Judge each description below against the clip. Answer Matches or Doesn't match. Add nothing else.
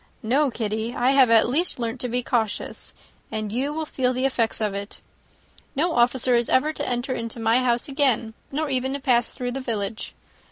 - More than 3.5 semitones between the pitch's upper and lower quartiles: Doesn't match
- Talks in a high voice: Matches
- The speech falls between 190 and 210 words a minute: Matches